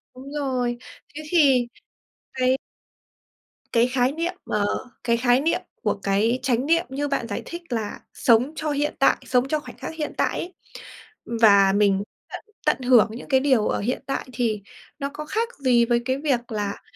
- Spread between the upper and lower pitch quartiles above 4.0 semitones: No, average, 3.5 semitones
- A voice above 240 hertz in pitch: Yes, very high, 255 Hz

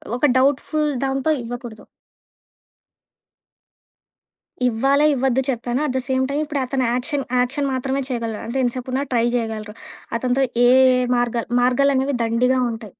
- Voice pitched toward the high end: Yes, very high, 255 Hz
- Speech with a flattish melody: Yes, narrow, 2.3 semitones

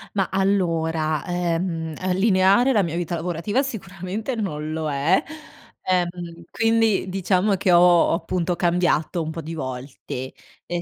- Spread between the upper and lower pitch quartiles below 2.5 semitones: No, average, 2.8 semitones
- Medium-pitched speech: Yes, medium, 175 Hz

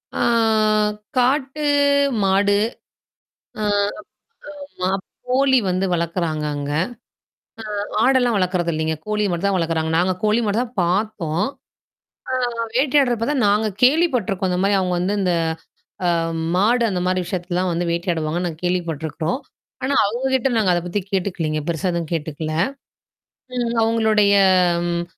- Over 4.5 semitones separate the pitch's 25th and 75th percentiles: Yes, average, 5.0 semitones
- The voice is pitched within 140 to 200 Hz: Yes, medium, 185 Hz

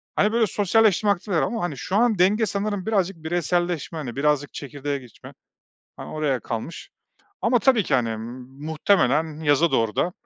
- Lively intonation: Yes, wide, 5.9 semitones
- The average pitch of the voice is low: No, medium, 170 Hz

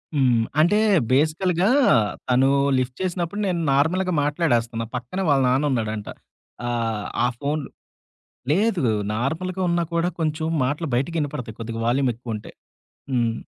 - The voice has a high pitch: No, medium, 140 Hz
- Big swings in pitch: Yes, wide, 5.9 semitones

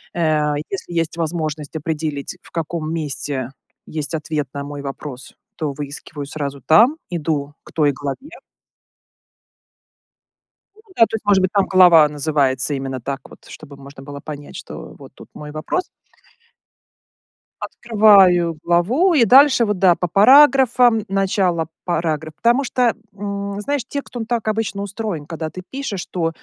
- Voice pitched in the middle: Yes, medium, 165 Hz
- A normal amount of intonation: No, wide, 5.9 semitones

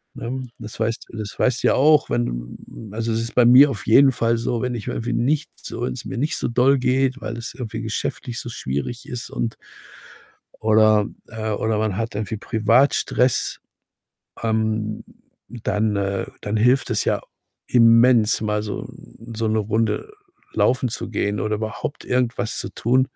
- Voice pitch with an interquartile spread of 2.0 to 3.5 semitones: Yes, narrow, 2.5 semitones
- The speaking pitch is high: No, low, 115 Hz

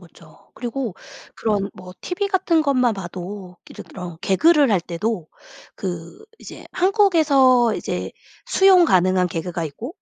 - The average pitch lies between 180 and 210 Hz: No, high, 220 Hz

